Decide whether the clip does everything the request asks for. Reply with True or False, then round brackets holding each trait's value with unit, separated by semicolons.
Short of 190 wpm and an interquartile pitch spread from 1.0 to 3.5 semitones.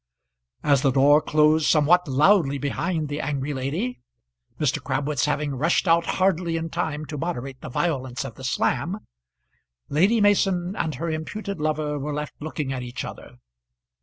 True (160 wpm; 3.1 semitones)